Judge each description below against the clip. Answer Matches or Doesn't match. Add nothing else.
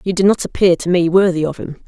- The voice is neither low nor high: Matches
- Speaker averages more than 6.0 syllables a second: Matches